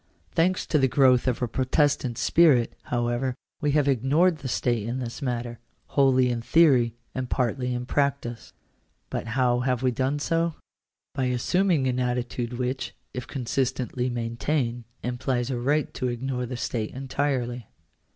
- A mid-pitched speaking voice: No, low, 125 Hz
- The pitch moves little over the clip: Yes, narrow, 2.2 semitones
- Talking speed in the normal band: Yes, average, 160 wpm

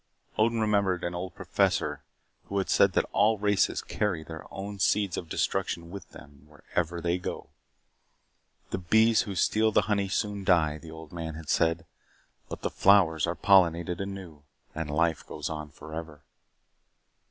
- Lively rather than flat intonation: No, average, 3.7 semitones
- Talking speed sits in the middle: Yes, average, 160 wpm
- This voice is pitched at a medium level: No, very low, 90 Hz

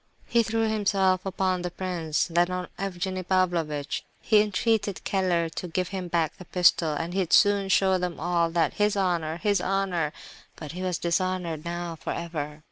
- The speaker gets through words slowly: No, average, 165 wpm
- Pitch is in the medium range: Yes, medium, 180 Hz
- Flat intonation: Yes, narrow, 2.3 semitones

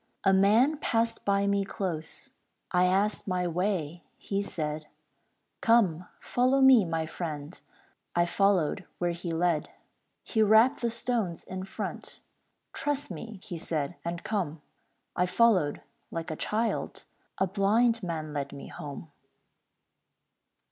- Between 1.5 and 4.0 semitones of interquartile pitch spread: No, average, 4.8 semitones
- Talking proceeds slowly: Yes, slow, 130 wpm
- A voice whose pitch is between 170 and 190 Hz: Yes, medium, 185 Hz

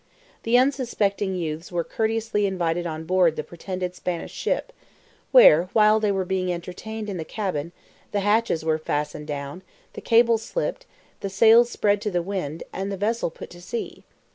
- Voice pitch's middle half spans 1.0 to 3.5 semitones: No, average, 4.4 semitones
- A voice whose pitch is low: No, high, 190 Hz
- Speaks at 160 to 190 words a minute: Yes, average, 170 wpm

